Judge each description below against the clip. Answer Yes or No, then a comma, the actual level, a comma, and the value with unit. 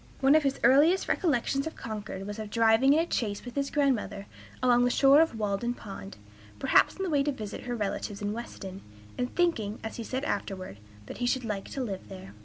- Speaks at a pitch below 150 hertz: No, high, 235 Hz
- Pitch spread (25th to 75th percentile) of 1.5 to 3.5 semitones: No, average, 5.1 semitones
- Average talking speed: No, fast, 215 wpm